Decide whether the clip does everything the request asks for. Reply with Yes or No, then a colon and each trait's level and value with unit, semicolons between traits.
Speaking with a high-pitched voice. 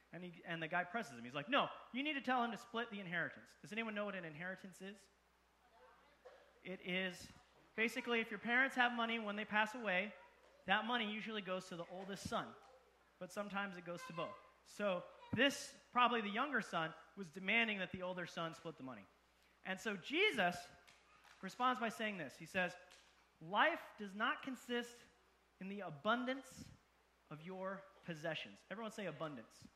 Yes: high, 200 Hz